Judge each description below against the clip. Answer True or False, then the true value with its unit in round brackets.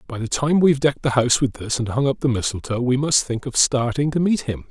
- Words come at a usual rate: False (295 wpm)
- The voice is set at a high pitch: False (130 Hz)